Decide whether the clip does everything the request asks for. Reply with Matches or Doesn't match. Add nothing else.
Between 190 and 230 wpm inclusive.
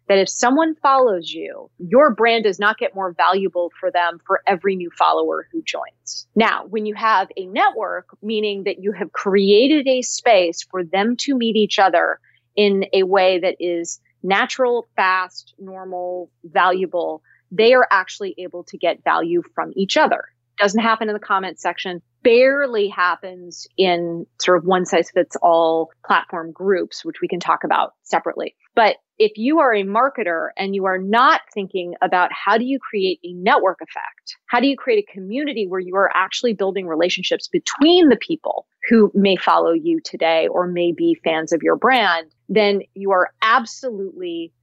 Doesn't match